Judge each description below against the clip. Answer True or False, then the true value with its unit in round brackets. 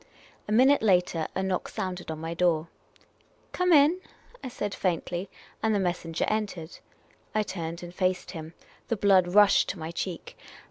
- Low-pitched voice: False (185 Hz)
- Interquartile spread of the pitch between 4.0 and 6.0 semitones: False (3.5 semitones)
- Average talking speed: True (175 wpm)